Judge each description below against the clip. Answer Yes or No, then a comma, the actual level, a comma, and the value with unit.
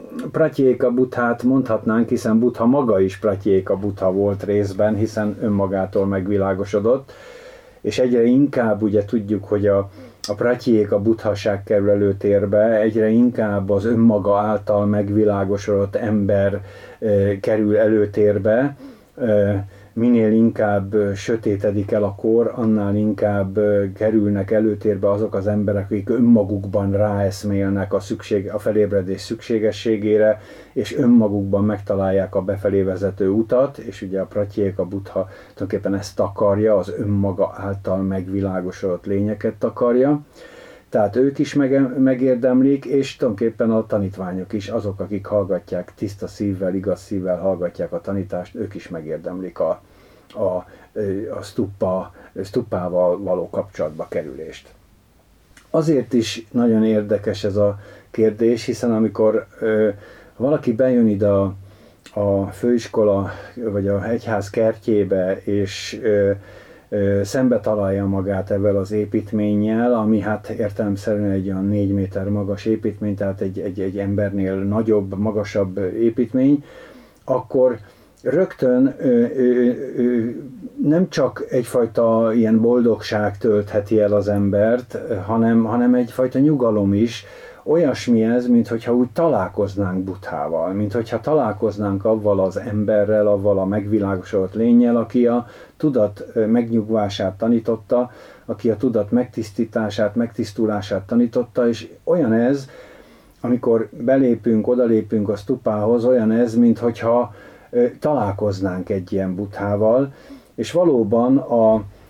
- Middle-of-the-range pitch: No, low, 105 Hz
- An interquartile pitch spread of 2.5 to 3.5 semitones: Yes, average, 2.8 semitones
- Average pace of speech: Yes, average, 120 wpm